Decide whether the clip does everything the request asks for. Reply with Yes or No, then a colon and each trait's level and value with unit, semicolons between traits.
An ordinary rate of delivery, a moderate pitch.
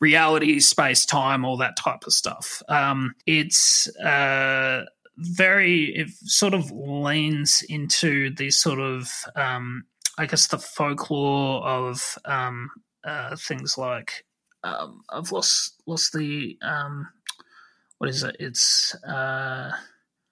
No: slow, 120 wpm; medium, 145 Hz